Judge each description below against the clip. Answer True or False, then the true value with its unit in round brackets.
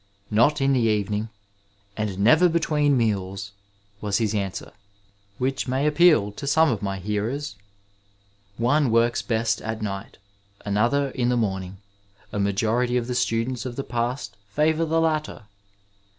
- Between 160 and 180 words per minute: False (150 wpm)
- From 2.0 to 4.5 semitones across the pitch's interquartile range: False (5.1 semitones)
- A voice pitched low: True (115 Hz)